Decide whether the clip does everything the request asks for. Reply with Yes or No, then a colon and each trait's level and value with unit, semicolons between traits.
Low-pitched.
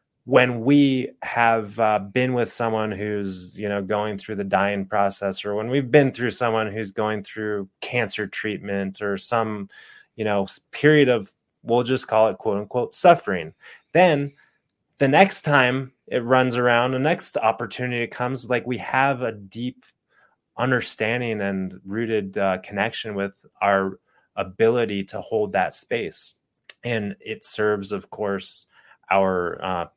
Yes: low, 110 Hz